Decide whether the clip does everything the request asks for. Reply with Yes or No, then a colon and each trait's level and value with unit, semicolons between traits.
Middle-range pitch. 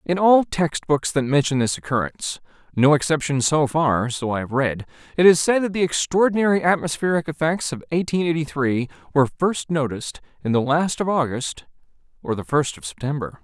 Yes: medium, 150 Hz